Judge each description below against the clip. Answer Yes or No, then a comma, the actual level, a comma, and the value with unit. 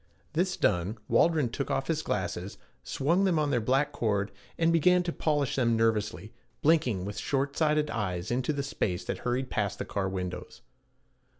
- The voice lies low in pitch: Yes, low, 130 Hz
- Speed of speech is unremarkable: Yes, average, 175 wpm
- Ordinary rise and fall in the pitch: No, wide, 6.9 semitones